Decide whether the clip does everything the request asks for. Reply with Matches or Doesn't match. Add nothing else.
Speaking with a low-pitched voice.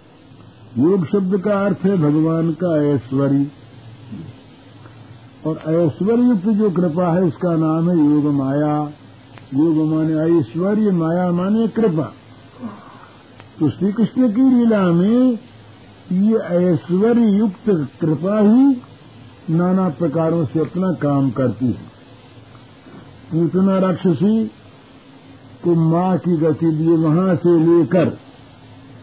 Doesn't match